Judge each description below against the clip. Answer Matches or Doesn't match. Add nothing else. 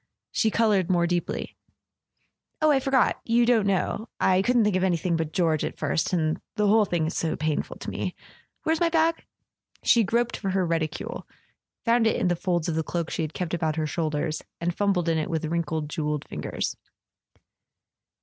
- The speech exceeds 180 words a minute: Matches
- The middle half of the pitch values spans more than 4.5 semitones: Matches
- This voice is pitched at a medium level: Matches